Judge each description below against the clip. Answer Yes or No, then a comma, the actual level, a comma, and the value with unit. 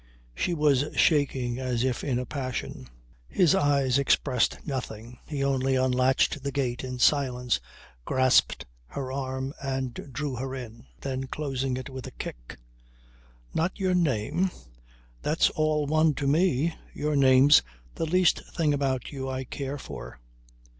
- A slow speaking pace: No, average, 145 wpm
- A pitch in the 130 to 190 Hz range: Yes, low, 135 Hz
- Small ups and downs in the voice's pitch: Yes, narrow, 2.3 semitones